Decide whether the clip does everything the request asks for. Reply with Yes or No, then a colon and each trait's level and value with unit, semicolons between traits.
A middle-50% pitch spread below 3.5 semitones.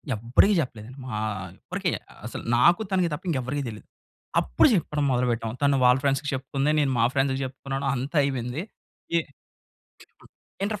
Yes: average, 2.9 semitones